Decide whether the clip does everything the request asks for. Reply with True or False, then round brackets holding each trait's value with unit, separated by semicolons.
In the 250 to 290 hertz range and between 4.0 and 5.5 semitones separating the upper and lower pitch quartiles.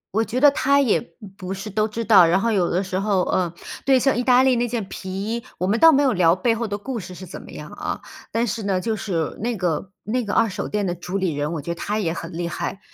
False (205 Hz; 4.3 semitones)